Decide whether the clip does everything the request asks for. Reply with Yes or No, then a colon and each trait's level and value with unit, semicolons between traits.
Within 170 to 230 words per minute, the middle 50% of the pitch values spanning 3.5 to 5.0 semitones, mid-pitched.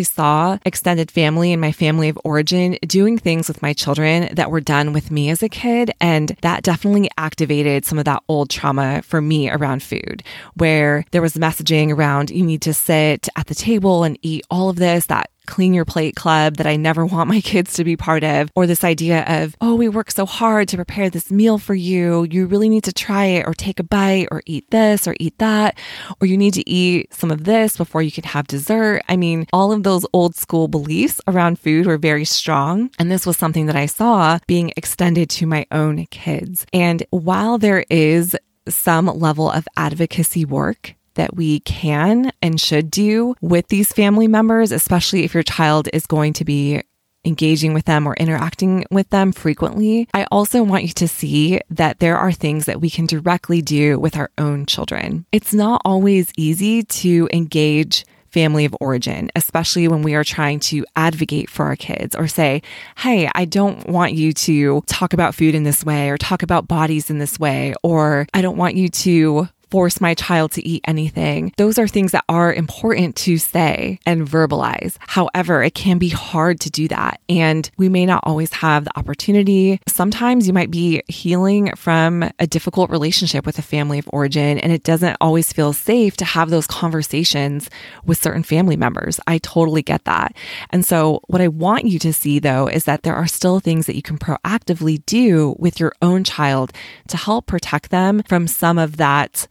No: average, 200 wpm; average, 2.9 semitones; medium, 165 Hz